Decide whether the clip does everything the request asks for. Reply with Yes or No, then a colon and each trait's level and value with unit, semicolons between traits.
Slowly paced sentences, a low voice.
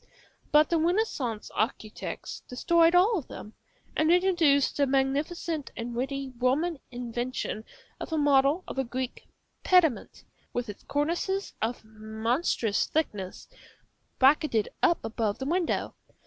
No: slow, 125 wpm; very high, 275 Hz